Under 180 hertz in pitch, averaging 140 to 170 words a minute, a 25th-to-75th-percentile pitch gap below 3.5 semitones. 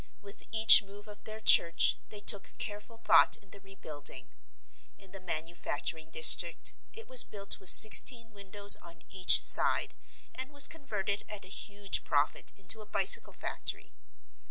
No: high, 200 Hz; average, 155 wpm; narrow, 2.6 semitones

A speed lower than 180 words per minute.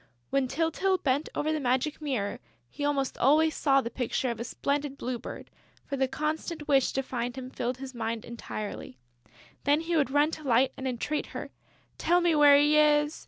No: average, 195 wpm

